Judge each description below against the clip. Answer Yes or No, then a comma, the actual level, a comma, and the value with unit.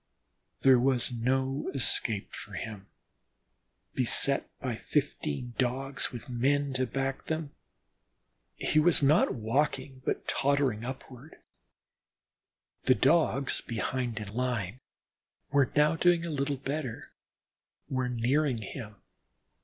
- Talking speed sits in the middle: No, slow, 110 wpm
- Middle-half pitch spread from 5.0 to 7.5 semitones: No, average, 2.8 semitones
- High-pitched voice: No, low, 130 Hz